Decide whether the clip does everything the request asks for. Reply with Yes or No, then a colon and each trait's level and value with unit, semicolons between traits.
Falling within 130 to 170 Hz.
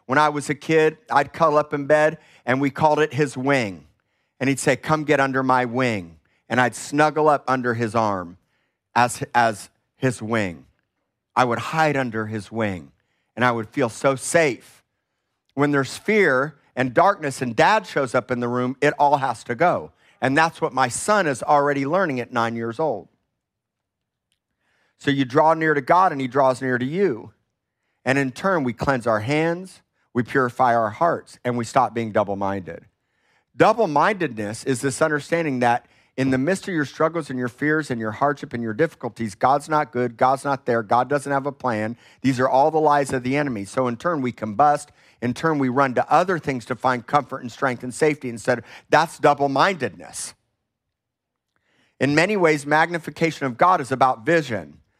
Yes: low, 135 Hz